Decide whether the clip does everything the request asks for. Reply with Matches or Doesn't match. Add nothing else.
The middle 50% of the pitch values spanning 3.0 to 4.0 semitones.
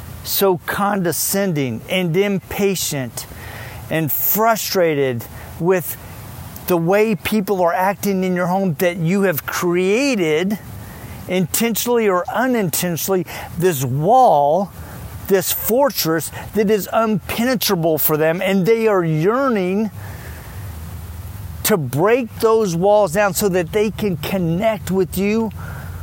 Doesn't match